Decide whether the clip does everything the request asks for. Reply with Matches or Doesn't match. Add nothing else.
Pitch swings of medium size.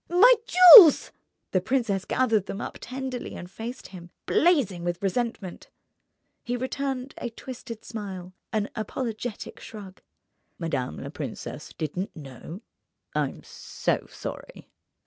Doesn't match